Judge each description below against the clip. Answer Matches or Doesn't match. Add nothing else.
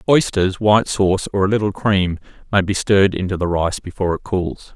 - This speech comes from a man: Matches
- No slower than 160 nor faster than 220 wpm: Matches